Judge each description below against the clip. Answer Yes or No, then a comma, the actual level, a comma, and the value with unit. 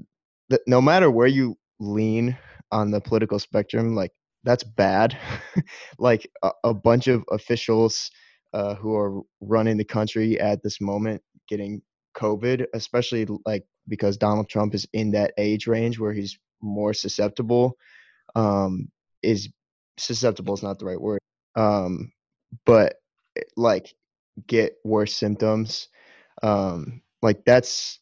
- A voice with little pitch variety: Yes, narrow, 2.1 semitones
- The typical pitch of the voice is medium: No, low, 110 Hz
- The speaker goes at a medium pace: No, slow, 130 wpm